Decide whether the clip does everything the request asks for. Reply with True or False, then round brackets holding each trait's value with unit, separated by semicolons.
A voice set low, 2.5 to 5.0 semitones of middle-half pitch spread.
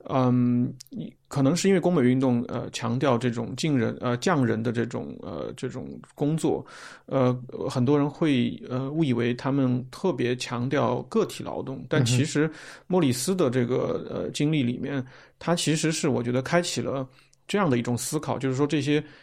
True (130 Hz; 3.3 semitones)